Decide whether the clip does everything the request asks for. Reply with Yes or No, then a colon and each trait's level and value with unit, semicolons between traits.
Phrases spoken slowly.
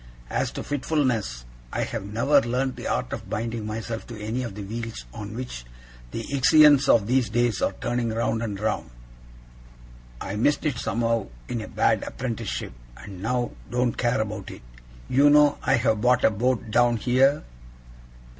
No: average, 170 wpm